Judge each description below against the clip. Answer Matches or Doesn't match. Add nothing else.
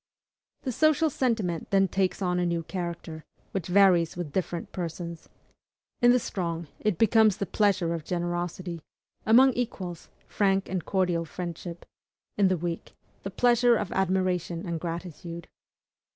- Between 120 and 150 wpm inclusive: Matches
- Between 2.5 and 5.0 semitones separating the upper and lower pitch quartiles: Matches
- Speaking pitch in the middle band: Matches